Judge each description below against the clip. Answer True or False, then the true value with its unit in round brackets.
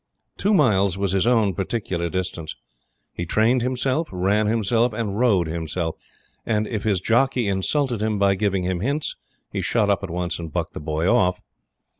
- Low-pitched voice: True (100 Hz)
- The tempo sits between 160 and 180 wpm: True (175 wpm)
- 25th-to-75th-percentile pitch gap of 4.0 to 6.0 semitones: True (4.3 semitones)